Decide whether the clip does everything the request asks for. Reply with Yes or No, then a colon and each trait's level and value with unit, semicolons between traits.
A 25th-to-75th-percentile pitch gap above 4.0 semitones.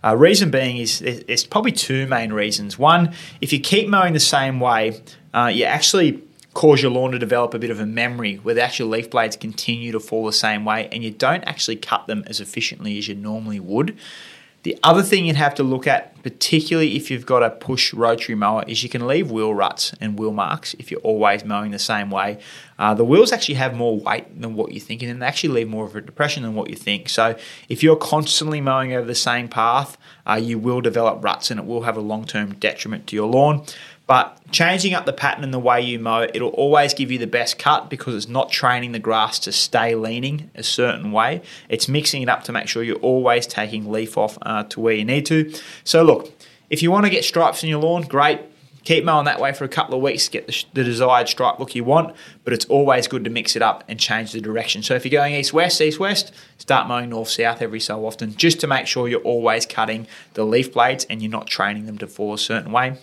Yes: average, 4.6 semitones